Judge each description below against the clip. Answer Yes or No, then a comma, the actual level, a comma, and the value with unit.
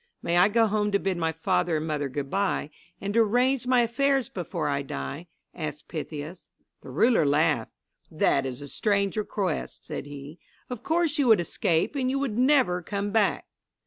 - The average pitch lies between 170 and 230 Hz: Yes, high, 190 Hz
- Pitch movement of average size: No, wide, 7.0 semitones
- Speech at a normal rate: Yes, average, 185 wpm